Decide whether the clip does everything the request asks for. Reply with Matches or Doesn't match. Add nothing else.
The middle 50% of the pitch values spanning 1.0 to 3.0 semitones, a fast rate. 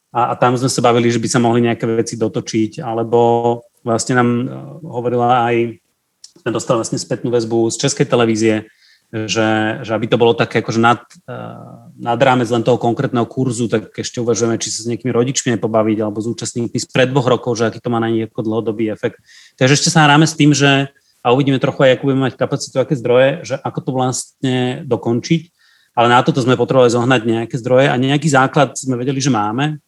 Matches